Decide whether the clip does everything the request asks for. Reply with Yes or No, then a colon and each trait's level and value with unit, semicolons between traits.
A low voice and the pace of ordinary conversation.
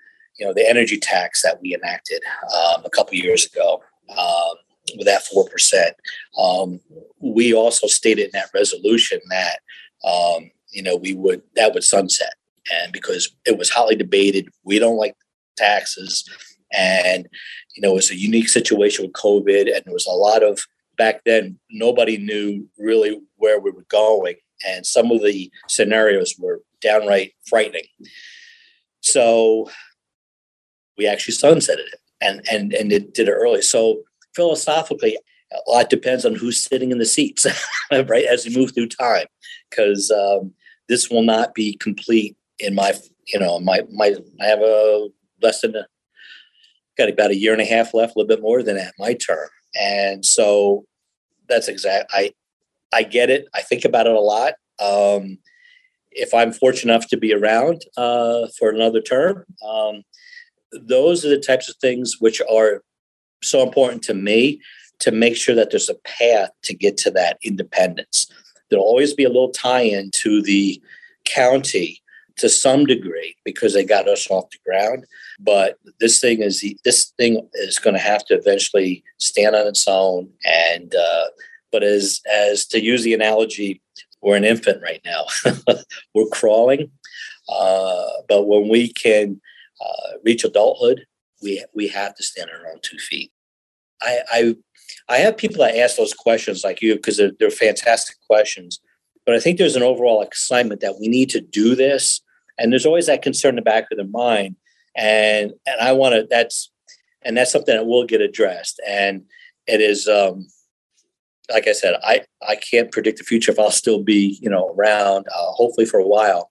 Yes: low, 120 Hz; average, 175 wpm